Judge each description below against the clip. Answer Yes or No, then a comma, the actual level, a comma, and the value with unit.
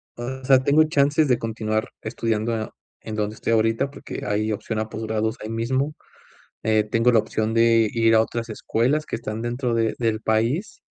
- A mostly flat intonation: Yes, narrow, 2.2 semitones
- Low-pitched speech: Yes, low, 115 Hz